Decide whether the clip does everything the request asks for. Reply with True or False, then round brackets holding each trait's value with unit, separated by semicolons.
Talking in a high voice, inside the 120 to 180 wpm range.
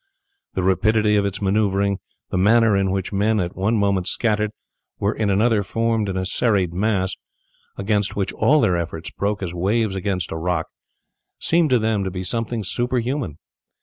False (100 Hz; 175 wpm)